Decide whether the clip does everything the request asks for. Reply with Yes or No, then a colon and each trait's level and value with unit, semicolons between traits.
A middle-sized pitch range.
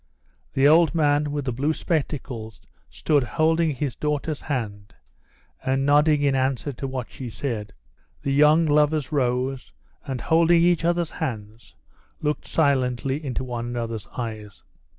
Yes: average, 3.7 semitones